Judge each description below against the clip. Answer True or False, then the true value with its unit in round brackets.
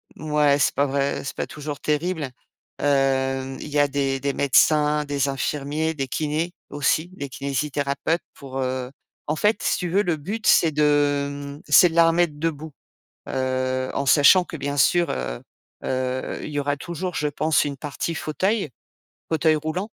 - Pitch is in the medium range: True (145 Hz)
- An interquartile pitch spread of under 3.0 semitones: True (2.4 semitones)